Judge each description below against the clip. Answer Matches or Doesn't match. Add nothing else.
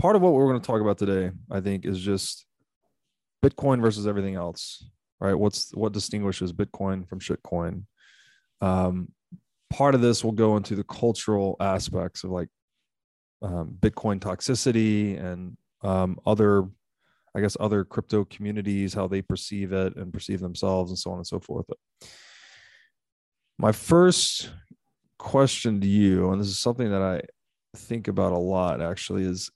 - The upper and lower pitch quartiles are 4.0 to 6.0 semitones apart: Doesn't match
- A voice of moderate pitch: Doesn't match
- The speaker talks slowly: Doesn't match